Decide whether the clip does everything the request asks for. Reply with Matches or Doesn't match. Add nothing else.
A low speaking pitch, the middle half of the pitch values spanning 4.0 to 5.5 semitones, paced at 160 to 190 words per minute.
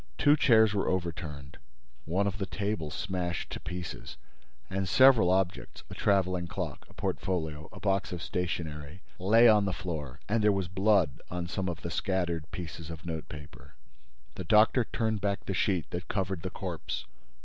Doesn't match